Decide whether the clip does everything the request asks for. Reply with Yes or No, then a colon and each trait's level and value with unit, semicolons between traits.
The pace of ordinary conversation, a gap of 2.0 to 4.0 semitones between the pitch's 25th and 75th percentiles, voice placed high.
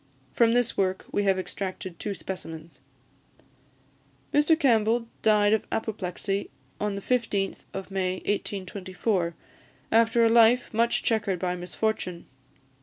No: slow, 120 wpm; average, 3.4 semitones; high, 200 Hz